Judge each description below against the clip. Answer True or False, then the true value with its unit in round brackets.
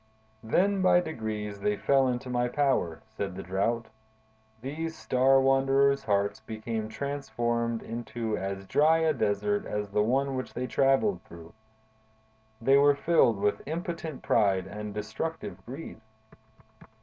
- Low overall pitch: True (120 Hz)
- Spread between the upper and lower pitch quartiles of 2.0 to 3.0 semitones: False (4.8 semitones)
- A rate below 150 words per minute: True (135 wpm)